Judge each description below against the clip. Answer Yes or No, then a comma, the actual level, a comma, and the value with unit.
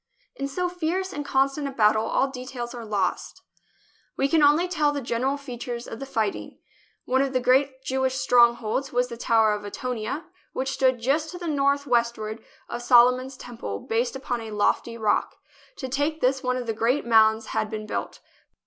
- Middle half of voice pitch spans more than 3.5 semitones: No, average, 3.1 semitones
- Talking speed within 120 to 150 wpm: No, average, 185 wpm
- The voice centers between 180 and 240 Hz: No, very high, 255 Hz